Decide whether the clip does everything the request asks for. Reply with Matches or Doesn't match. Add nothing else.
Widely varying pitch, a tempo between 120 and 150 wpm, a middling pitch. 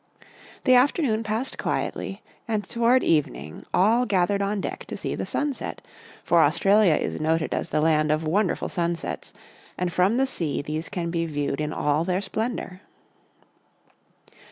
Doesn't match